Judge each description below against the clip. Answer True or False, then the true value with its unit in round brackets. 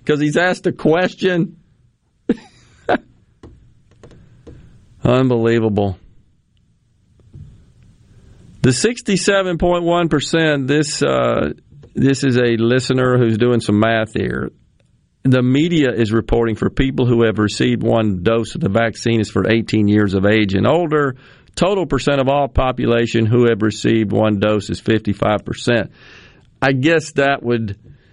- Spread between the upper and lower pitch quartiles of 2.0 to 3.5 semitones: False (4.3 semitones)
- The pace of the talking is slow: True (130 wpm)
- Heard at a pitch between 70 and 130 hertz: True (120 Hz)